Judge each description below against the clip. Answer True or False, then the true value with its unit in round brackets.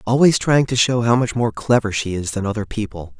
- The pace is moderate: False (245 wpm)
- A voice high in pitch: False (115 Hz)